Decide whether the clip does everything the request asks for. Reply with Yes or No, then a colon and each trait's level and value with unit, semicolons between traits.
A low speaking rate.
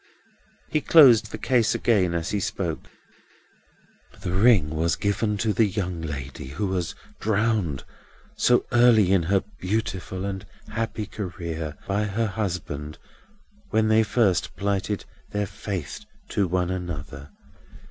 Yes: slow, 130 wpm